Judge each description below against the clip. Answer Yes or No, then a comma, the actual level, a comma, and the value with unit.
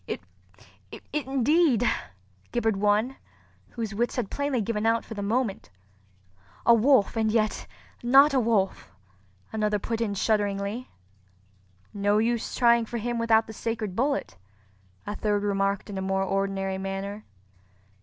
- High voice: Yes, high, 215 Hz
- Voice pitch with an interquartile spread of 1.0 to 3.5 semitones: Yes, average, 3.0 semitones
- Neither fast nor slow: No, slow, 130 wpm